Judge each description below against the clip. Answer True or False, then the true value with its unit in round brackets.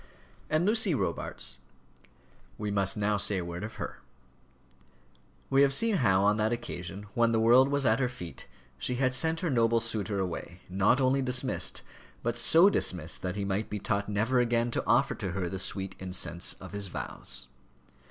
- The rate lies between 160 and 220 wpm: True (180 wpm)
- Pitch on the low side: True (110 Hz)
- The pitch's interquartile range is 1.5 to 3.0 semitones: False (4.8 semitones)